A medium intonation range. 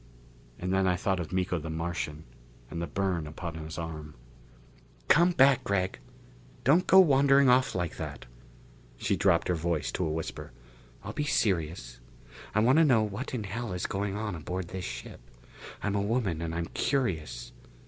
No: wide, 5.9 semitones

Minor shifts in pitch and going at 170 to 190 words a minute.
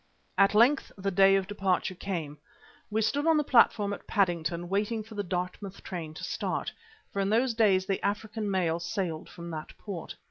No: average, 3.2 semitones; average, 185 wpm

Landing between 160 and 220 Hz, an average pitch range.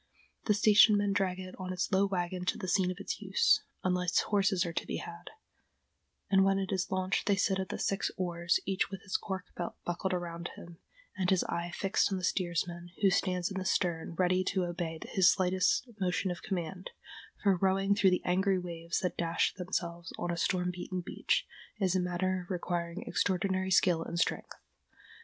No: medium, 185 Hz; narrow, 1.6 semitones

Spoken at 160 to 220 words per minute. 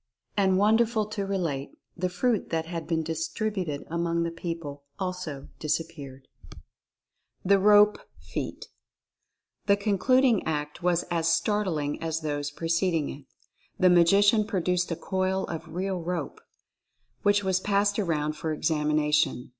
No: slow, 135 wpm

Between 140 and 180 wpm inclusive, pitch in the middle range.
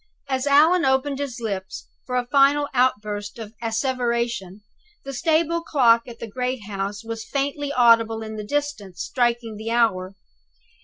No: average, 150 wpm; high, 240 Hz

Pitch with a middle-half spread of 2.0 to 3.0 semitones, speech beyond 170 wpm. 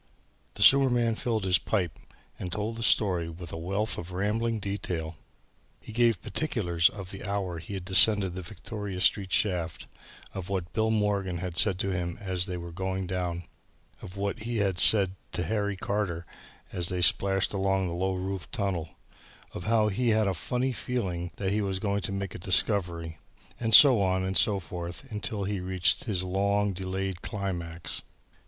Yes: narrow, 2.6 semitones; average, 180 wpm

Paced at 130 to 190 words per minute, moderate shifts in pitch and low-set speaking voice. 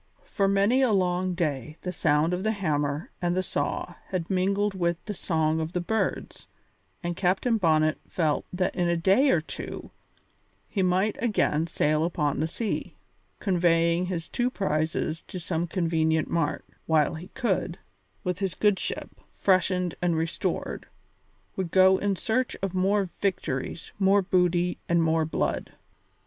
No: average, 155 wpm; average, 3.0 semitones; medium, 180 Hz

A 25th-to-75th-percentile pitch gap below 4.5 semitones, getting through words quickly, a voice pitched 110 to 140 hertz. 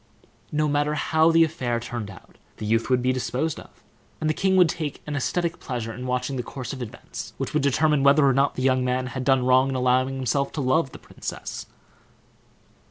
Yes: average, 3.0 semitones; fast, 215 wpm; low, 135 Hz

